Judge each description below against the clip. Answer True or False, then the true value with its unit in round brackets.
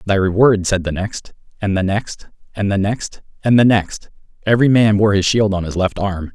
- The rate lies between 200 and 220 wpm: False (190 wpm)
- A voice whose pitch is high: False (100 Hz)